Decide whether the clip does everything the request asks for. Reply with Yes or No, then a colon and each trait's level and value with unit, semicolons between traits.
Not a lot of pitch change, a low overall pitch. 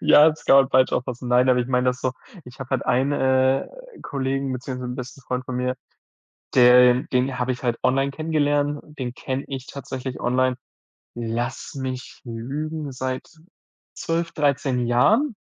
Yes: narrow, 1.7 semitones; low, 130 Hz